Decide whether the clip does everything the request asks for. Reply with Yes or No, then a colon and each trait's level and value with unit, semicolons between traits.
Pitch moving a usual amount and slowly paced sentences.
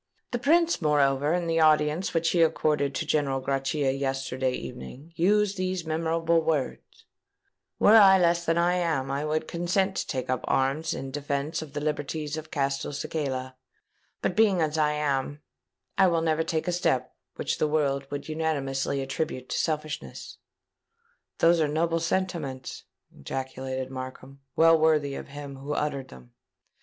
No: average, 3.3 semitones; average, 155 wpm